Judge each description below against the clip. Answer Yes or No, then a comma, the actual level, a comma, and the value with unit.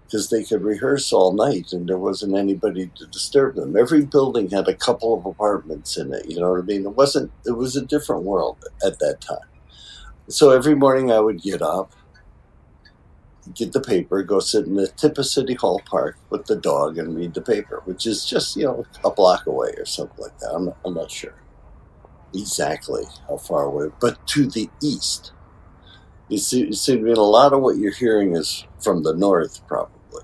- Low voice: Yes, low, 125 Hz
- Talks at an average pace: Yes, average, 205 wpm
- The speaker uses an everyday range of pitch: No, wide, 6.7 semitones